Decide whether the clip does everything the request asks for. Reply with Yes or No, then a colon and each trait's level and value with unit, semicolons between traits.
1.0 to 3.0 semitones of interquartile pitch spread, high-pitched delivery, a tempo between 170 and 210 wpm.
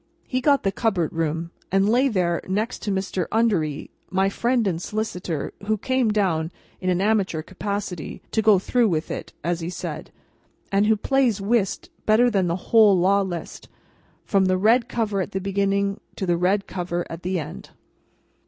No: average, 3.4 semitones; high, 195 Hz; average, 180 wpm